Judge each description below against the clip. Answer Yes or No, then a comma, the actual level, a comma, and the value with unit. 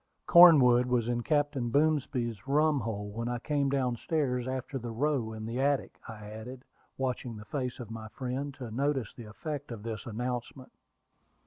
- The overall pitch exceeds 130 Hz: No, low, 125 Hz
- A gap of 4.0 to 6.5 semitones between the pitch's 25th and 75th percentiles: No, average, 3.4 semitones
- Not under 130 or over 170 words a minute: Yes, average, 165 wpm